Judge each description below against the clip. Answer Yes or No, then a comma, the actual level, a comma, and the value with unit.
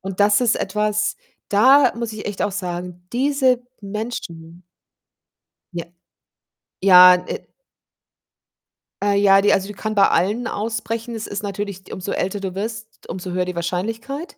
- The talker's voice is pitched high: Yes, high, 205 Hz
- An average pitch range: Yes, average, 3.3 semitones